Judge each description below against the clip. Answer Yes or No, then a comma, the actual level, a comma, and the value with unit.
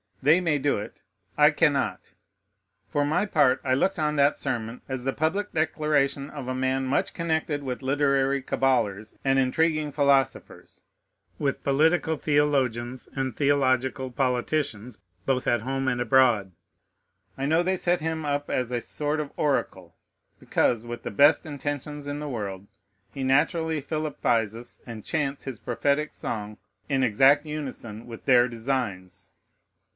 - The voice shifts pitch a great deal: No, average, 3.1 semitones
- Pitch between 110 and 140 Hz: Yes, low, 135 Hz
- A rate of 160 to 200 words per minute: No, average, 145 wpm